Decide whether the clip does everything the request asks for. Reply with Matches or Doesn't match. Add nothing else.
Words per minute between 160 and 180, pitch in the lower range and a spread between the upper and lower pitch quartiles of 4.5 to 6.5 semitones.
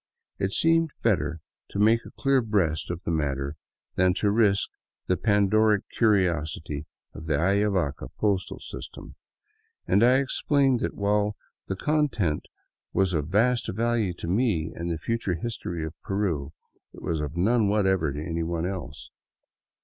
Doesn't match